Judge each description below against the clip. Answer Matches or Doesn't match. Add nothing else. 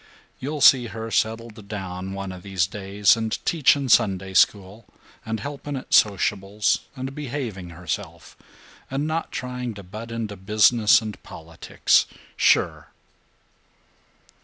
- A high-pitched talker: Doesn't match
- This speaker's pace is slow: Matches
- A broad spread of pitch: Doesn't match